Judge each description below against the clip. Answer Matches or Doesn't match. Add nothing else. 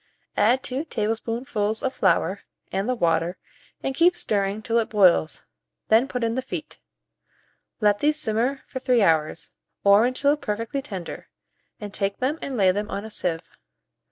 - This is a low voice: Doesn't match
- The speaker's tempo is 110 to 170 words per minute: Matches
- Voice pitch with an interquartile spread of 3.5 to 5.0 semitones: Matches